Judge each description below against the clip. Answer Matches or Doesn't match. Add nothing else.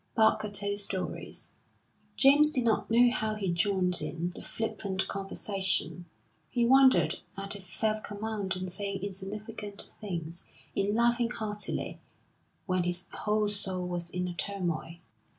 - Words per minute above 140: Doesn't match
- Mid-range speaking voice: Doesn't match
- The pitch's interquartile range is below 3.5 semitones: Matches